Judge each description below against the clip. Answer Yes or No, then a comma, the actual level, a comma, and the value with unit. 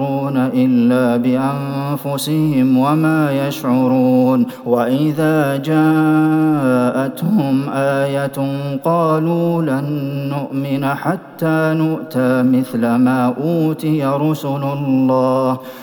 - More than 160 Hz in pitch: No, medium, 140 Hz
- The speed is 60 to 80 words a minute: Yes, slow, 65 wpm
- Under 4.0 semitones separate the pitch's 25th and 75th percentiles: Yes, average, 3.2 semitones